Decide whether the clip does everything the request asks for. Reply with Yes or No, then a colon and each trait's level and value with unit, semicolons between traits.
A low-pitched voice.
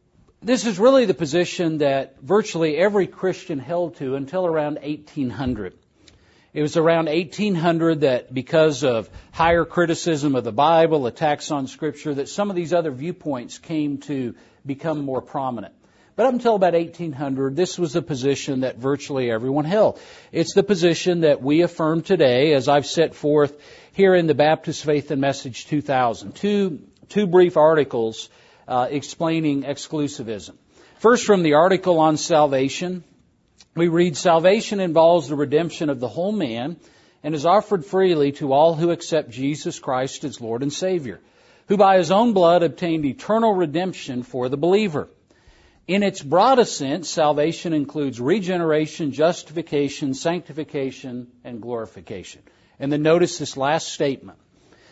No: medium, 155 Hz